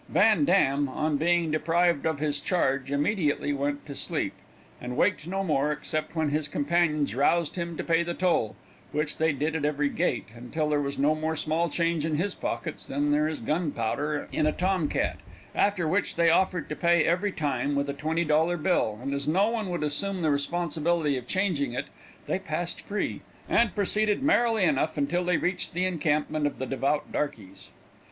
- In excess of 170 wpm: Yes, average, 190 wpm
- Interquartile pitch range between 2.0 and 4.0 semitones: Yes, average, 3.3 semitones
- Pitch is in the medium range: Yes, medium, 155 Hz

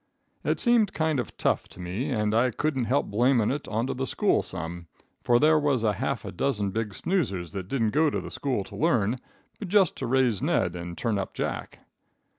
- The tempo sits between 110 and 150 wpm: No, fast, 205 wpm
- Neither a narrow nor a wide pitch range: No, wide, 6.3 semitones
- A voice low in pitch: Yes, low, 120 Hz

